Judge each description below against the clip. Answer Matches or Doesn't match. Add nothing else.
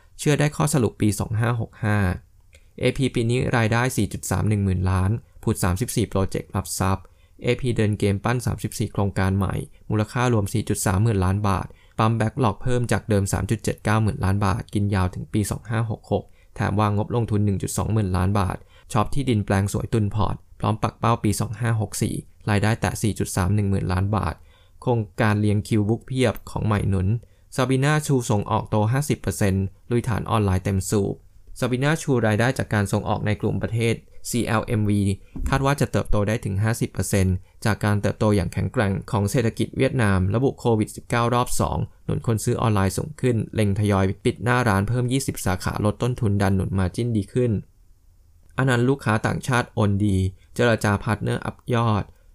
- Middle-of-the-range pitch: Doesn't match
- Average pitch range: Matches